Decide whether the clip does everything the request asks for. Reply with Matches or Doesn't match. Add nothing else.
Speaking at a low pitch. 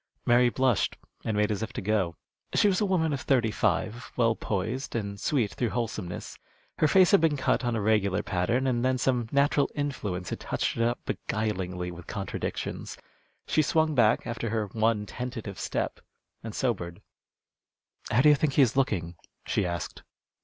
Matches